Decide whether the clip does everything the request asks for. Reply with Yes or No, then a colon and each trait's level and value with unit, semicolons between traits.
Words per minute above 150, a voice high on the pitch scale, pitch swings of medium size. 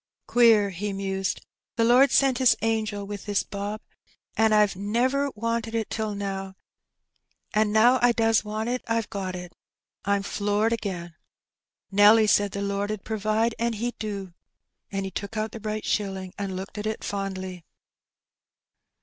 No: average, 170 wpm; high, 210 Hz; narrow, 2.2 semitones